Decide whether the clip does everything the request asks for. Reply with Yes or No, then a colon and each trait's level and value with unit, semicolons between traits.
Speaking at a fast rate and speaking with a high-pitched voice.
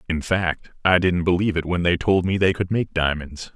No: fast, 235 wpm; very low, 90 Hz